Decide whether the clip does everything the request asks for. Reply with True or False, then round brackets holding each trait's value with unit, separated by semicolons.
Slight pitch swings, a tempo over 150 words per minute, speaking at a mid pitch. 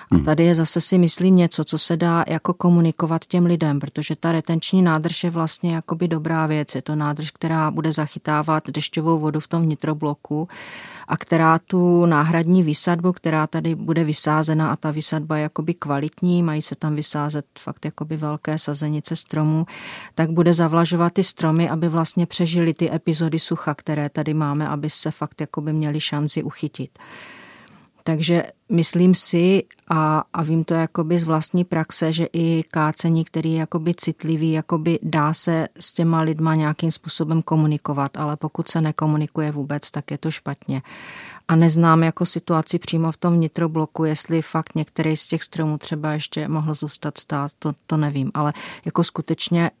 True (1.6 semitones; 170 wpm; 160 Hz)